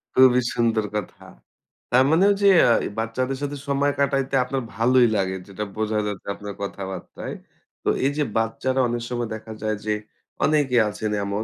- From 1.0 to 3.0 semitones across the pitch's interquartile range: No, average, 3.7 semitones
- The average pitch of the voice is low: Yes, low, 120 Hz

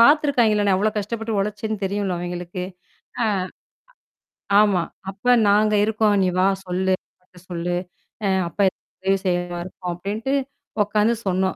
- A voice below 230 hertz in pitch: Yes, high, 200 Hz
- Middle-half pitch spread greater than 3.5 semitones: No, average, 2.9 semitones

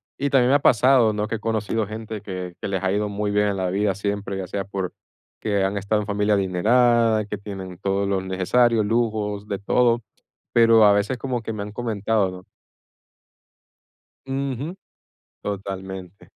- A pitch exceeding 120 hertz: No, low, 105 Hz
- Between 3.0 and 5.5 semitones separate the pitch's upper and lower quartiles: No, narrow, 2.6 semitones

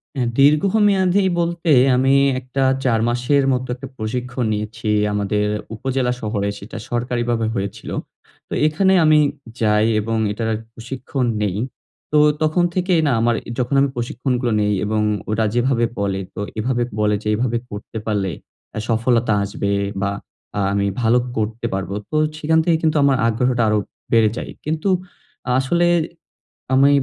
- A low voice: Yes, low, 120 Hz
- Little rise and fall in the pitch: No, average, 4.4 semitones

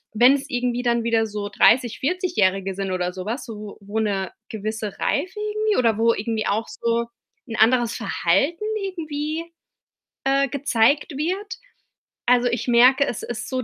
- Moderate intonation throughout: Yes, average, 4.7 semitones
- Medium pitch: No, high, 240 Hz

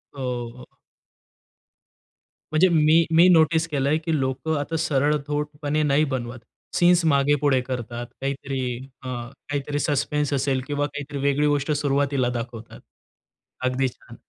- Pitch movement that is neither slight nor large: No, narrow, 2.3 semitones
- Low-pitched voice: No, medium, 145 Hz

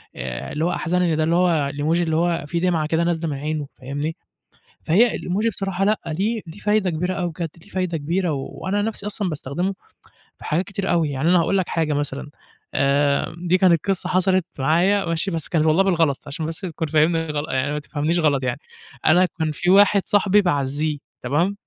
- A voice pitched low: No, medium, 165 Hz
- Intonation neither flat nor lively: Yes, average, 3.6 semitones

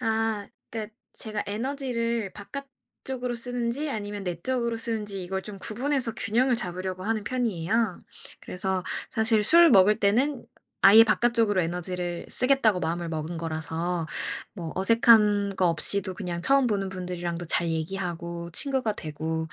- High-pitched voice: Yes, high, 205 Hz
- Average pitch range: Yes, average, 4.7 semitones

